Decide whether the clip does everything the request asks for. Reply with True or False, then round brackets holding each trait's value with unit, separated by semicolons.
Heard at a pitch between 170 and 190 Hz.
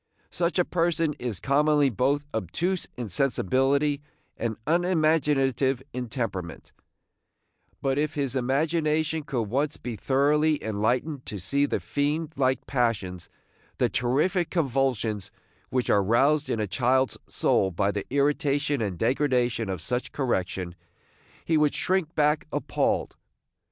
False (135 Hz)